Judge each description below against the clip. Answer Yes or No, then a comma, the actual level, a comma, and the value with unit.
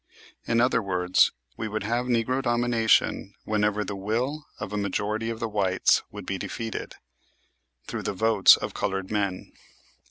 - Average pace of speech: Yes, average, 155 wpm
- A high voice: No, low, 110 Hz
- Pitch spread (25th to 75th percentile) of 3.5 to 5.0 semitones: No, narrow, 2.4 semitones